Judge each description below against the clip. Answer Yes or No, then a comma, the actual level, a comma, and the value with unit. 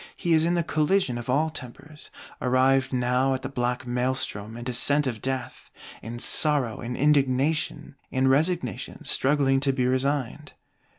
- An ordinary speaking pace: Yes, average, 155 wpm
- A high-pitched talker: No, low, 130 Hz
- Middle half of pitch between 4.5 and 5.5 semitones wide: No, average, 2.9 semitones